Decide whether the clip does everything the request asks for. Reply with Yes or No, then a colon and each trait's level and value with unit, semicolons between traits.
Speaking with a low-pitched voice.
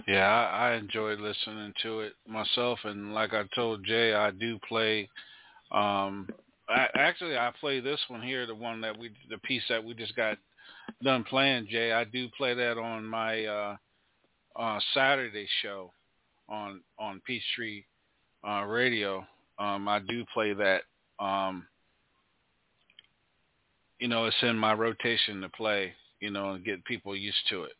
Yes: low, 110 Hz